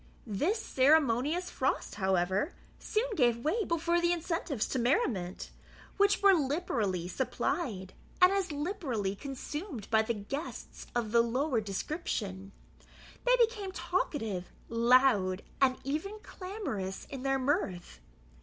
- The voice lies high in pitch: Yes, very high, 270 Hz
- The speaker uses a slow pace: Yes, slow, 120 wpm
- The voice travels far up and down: Yes, wide, 8.6 semitones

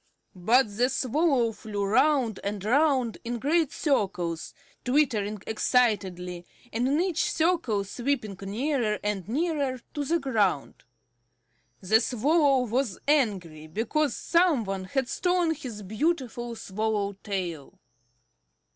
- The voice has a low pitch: No, high, 235 Hz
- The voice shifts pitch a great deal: Yes, wide, 5.9 semitones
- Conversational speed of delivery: No, slow, 115 wpm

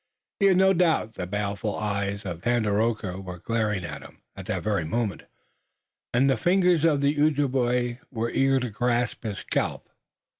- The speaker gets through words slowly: No, average, 175 wpm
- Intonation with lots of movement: No, average, 5.0 semitones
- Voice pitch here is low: Yes, low, 115 Hz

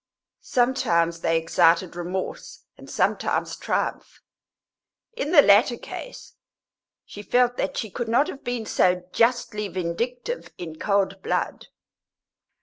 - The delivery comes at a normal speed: No, slow, 120 wpm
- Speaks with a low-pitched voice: No, high, 205 Hz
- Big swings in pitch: Yes, wide, 5.9 semitones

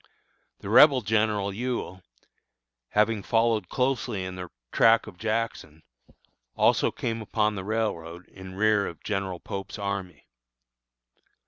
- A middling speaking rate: No, slow, 120 wpm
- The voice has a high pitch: No, low, 105 Hz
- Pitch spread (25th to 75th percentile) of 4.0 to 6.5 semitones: No, average, 3.1 semitones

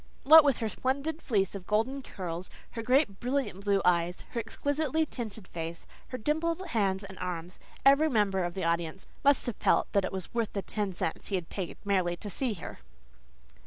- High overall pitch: Yes, high, 205 Hz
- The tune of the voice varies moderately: No, wide, 6.3 semitones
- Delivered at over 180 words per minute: Yes, average, 190 wpm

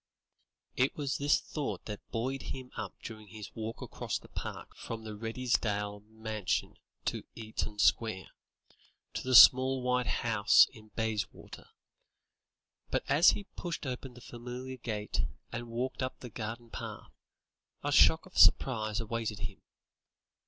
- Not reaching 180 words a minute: Yes, average, 140 wpm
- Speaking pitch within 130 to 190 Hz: No, low, 115 Hz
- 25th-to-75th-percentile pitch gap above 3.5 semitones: No, average, 2.9 semitones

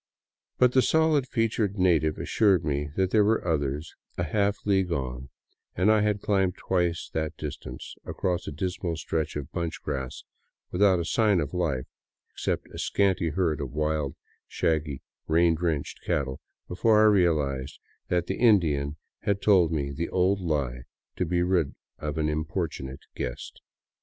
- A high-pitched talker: No, very low, 85 Hz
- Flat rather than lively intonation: No, average, 4.6 semitones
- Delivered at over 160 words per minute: No, average, 155 wpm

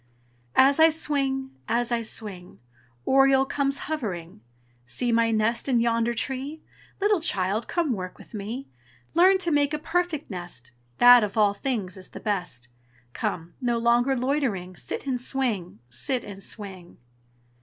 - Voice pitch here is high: Yes, high, 235 Hz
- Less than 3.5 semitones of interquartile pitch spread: No, wide, 5.5 semitones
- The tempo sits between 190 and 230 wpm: No, average, 150 wpm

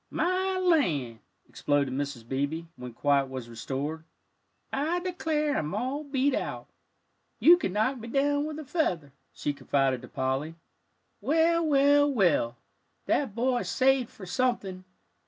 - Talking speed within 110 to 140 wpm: Yes, slow, 135 wpm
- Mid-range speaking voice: No, high, 225 Hz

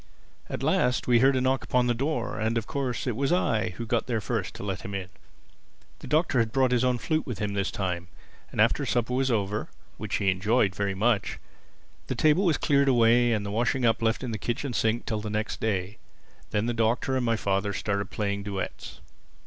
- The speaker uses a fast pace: Yes, fast, 220 wpm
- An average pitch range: Yes, average, 3.5 semitones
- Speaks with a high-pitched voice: No, low, 115 Hz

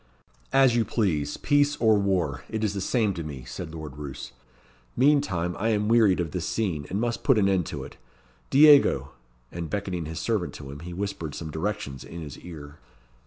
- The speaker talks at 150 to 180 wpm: No, average, 195 wpm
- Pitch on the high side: No, very low, 95 Hz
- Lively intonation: Yes, wide, 5.9 semitones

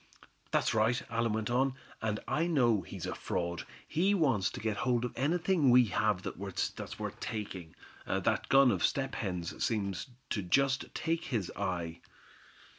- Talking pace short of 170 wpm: Yes, average, 160 wpm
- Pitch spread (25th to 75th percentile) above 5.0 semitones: Yes, wide, 5.4 semitones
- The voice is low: Yes, low, 115 Hz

